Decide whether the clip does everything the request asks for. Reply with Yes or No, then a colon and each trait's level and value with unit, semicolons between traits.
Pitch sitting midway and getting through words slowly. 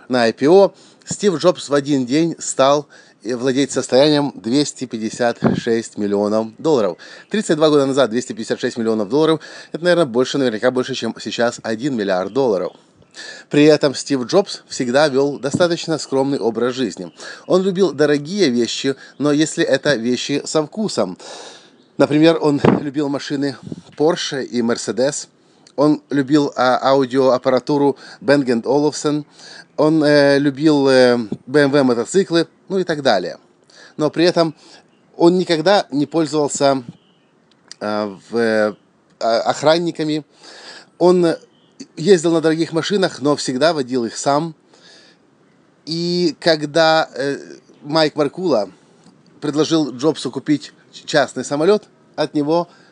Yes: medium, 145 Hz; slow, 120 wpm